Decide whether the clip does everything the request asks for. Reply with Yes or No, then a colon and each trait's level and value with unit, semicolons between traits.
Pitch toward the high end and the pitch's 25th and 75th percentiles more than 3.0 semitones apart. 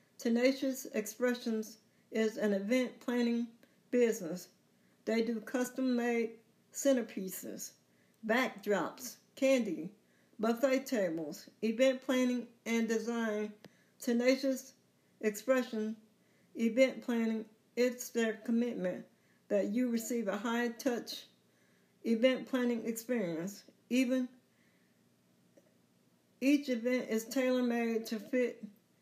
No: high, 235 Hz; average, 2.7 semitones